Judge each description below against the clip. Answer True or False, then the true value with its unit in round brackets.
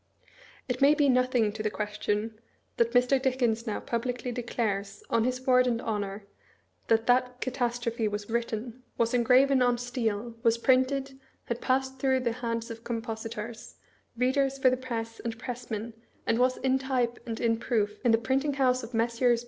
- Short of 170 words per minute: False (175 wpm)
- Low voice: False (240 Hz)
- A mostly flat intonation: True (2.1 semitones)